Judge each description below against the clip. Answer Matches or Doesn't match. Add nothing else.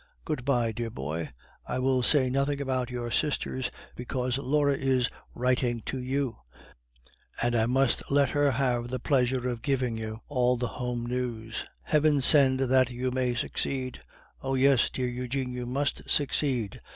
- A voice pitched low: Matches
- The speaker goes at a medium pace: Matches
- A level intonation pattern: Matches